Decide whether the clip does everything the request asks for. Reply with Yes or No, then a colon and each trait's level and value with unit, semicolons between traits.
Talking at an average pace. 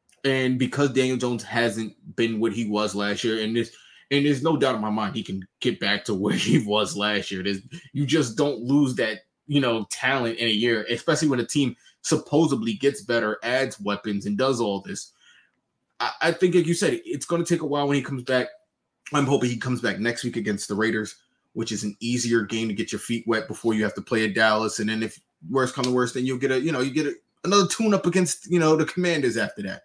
No: fast, 250 wpm